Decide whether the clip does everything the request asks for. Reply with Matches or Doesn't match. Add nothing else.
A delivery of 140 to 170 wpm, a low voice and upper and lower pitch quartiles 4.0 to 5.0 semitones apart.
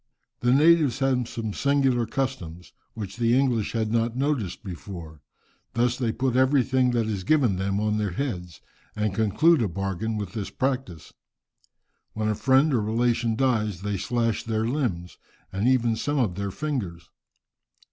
Matches